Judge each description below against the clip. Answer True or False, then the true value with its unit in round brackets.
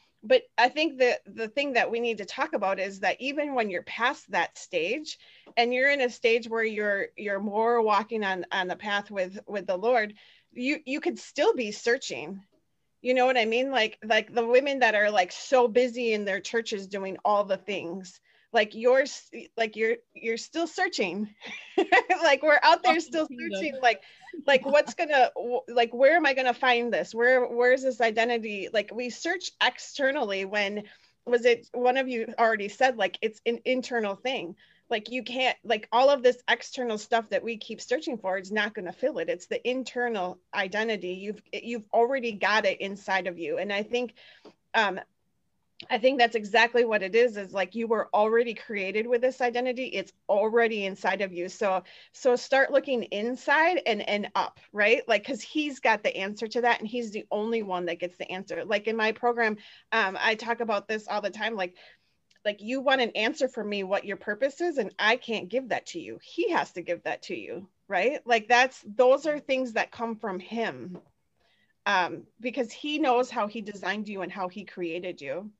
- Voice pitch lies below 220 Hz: False (230 Hz)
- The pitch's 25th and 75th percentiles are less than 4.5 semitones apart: True (3.8 semitones)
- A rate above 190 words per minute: True (200 wpm)